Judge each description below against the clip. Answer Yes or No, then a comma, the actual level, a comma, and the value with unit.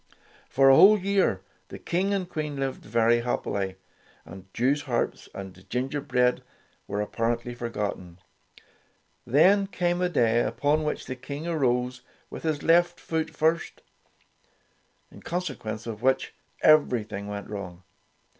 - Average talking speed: No, slow, 130 wpm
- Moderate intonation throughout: No, wide, 6.0 semitones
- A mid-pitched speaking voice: No, low, 130 Hz